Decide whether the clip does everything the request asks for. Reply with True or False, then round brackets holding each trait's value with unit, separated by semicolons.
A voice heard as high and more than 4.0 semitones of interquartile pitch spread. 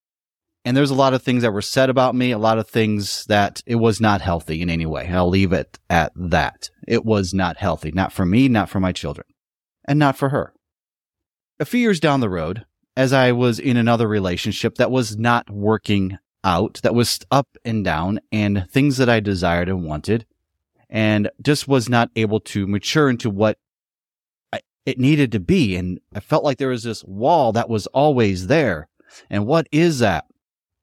False (110 Hz; 5.0 semitones)